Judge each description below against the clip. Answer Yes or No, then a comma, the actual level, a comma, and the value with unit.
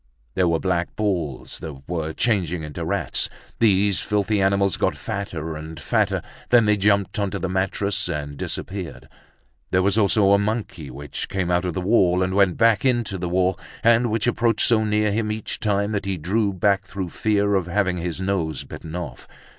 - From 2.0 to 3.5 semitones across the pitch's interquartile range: Yes, average, 2.9 semitones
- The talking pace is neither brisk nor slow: Yes, average, 185 wpm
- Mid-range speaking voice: No, very low, 95 Hz